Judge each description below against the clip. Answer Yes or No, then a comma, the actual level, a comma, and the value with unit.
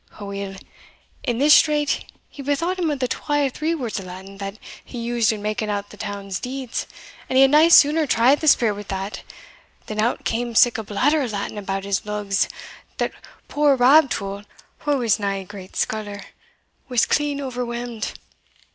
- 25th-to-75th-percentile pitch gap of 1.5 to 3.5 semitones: No, wide, 5.6 semitones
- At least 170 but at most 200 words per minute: Yes, average, 180 wpm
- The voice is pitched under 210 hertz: No, high, 235 Hz